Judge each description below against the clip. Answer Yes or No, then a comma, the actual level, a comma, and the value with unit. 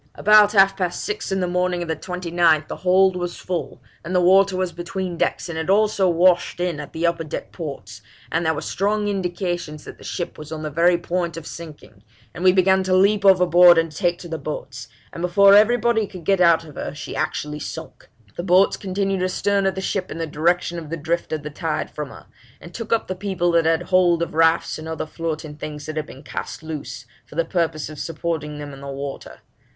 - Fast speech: Yes, fast, 230 wpm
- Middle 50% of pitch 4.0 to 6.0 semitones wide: No, average, 2.8 semitones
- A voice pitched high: No, medium, 175 Hz